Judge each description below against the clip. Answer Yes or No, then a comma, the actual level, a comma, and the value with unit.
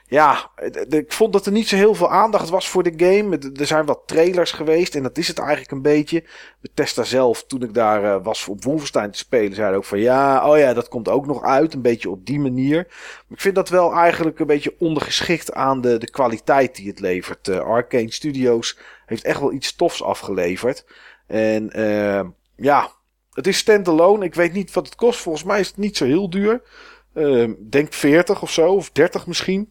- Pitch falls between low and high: Yes, medium, 160 Hz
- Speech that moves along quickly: Yes, fast, 220 wpm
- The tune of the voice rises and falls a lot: Yes, wide, 6.8 semitones